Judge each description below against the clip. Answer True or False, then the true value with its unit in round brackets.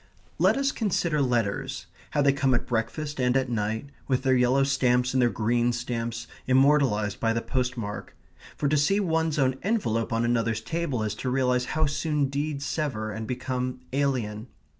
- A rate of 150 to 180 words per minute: True (175 wpm)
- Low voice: True (130 Hz)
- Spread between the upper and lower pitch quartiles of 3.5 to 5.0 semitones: True (3.8 semitones)